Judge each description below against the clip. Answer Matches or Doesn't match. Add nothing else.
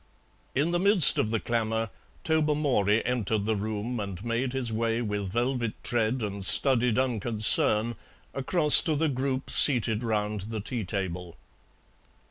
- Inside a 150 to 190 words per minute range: Doesn't match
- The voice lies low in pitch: Matches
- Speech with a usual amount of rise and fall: Matches